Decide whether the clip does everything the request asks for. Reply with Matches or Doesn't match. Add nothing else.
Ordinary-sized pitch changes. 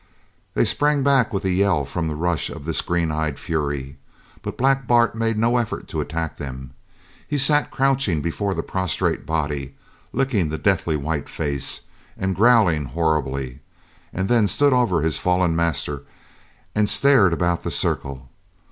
Doesn't match